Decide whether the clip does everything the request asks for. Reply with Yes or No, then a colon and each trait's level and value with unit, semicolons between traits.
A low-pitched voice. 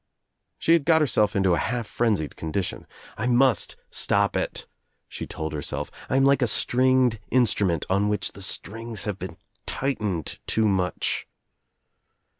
Yes: low, 110 Hz